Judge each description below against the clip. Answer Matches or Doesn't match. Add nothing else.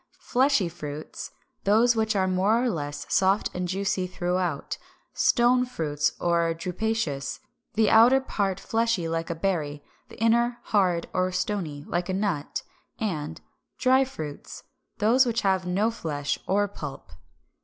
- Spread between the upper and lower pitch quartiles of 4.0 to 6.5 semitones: Matches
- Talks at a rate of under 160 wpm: Matches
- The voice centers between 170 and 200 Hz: Matches